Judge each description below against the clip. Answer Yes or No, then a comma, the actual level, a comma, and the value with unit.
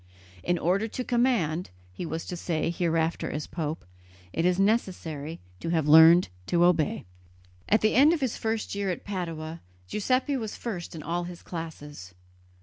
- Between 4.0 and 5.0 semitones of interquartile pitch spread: Yes, average, 4.5 semitones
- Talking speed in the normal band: Yes, average, 165 wpm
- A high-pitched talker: No, medium, 175 Hz